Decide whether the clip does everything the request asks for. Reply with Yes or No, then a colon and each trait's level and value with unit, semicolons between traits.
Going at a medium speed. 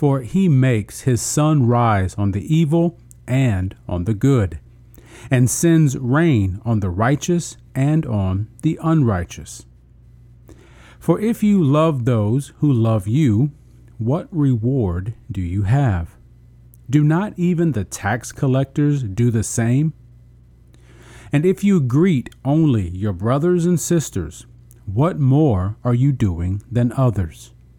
No: slow, 130 wpm